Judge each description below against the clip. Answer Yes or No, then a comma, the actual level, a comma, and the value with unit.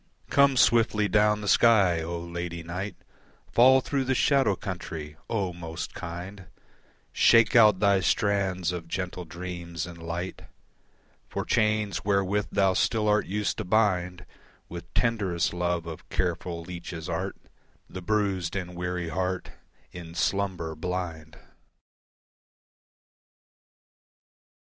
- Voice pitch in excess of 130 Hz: No, very low, 90 Hz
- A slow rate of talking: Yes, slow, 120 wpm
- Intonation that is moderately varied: Yes, average, 3.2 semitones